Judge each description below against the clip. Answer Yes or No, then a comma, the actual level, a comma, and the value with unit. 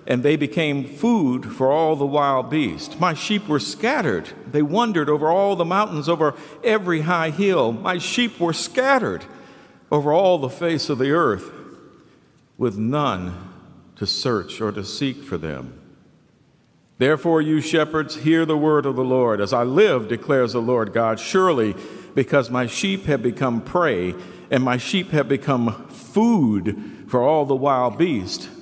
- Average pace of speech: Yes, average, 160 wpm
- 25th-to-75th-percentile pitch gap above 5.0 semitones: Yes, wide, 5.6 semitones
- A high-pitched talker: No, medium, 150 Hz